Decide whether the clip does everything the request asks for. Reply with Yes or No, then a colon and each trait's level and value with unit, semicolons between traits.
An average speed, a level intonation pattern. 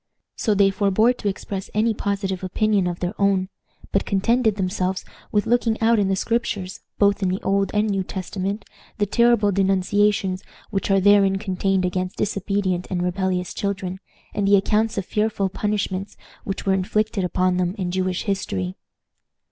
Yes: average, 165 wpm; narrow, 1.9 semitones